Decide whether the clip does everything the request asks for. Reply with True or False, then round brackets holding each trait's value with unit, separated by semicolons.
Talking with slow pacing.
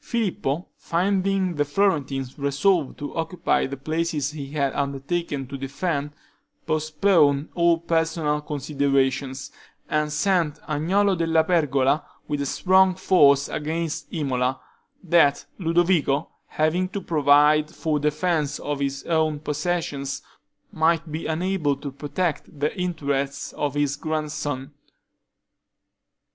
True (115 wpm)